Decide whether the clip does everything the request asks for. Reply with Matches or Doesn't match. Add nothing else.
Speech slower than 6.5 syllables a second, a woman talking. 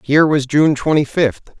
Doesn't match